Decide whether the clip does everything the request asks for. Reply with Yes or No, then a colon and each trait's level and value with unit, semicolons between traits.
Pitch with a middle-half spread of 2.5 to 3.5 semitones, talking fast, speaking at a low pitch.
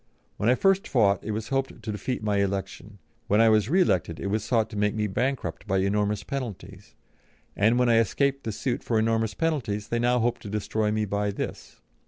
Yes: average, 3.0 semitones; fast, 215 wpm; low, 110 Hz